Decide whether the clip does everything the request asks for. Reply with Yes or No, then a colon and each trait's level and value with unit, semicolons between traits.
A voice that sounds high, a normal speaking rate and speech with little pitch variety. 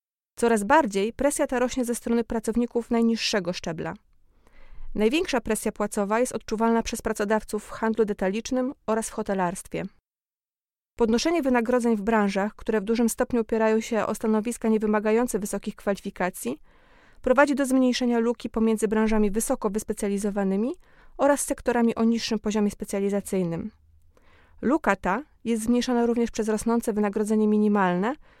Yes: high, 225 Hz; average, 130 wpm; narrow, 2.2 semitones